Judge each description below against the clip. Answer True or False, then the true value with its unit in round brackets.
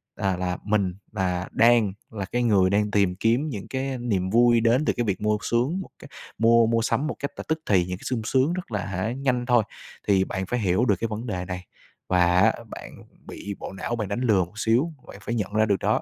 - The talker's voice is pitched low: True (110 Hz)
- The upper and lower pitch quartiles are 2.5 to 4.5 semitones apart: True (4.0 semitones)